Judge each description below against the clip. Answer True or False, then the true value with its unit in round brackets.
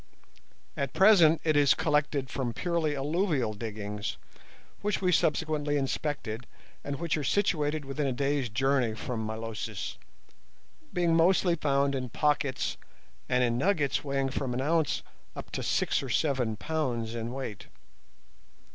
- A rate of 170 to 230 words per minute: False (140 wpm)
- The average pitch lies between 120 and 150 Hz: True (140 Hz)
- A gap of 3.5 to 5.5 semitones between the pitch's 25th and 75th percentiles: True (4.1 semitones)